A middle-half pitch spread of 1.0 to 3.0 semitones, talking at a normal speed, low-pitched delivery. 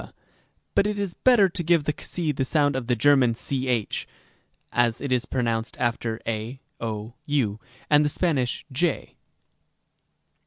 No: average, 4.4 semitones; average, 160 wpm; low, 130 Hz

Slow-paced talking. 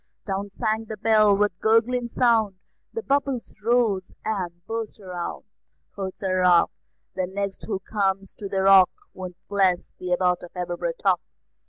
No: average, 155 wpm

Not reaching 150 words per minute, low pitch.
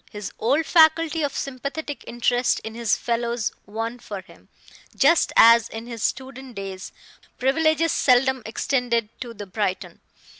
No: average, 140 wpm; high, 240 Hz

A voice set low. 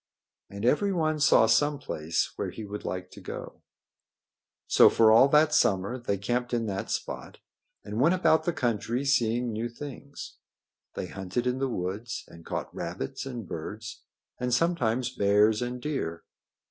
Yes: low, 120 Hz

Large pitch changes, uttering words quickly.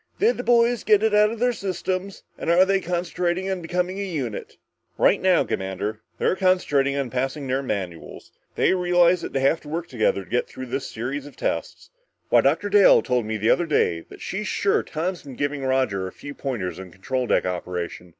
Yes: wide, 7.4 semitones; fast, 210 wpm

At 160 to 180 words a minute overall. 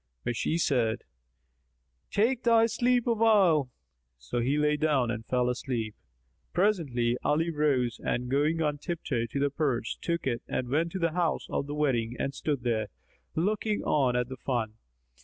Yes: average, 165 wpm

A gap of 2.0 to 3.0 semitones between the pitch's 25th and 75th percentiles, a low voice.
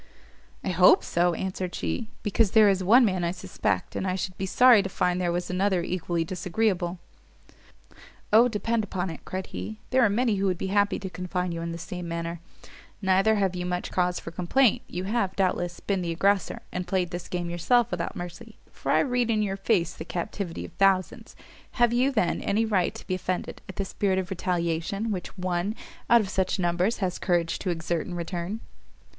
No: narrow, 2.6 semitones; medium, 185 Hz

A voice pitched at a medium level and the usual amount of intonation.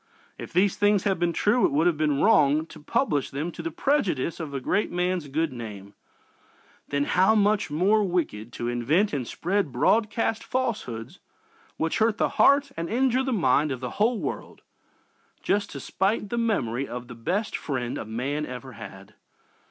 No: medium, 165 Hz; wide, 7.9 semitones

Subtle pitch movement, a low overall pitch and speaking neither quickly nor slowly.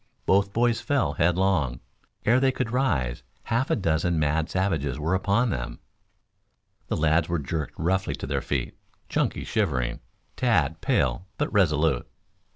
No: wide, 5.5 semitones; very low, 85 Hz; average, 145 wpm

